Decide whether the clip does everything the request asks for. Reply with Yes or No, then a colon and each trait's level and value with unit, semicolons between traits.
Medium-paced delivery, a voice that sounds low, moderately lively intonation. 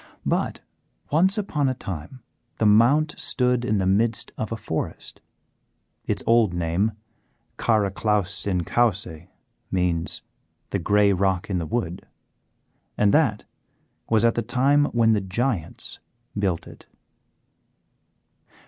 No: slow, 120 wpm; low, 105 Hz; average, 4.4 semitones